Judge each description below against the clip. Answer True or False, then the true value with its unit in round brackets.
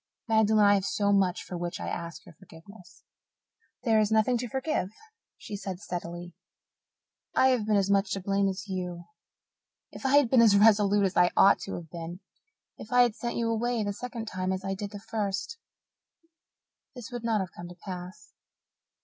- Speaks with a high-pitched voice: True (200 Hz)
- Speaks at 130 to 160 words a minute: False (190 wpm)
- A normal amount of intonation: True (3.3 semitones)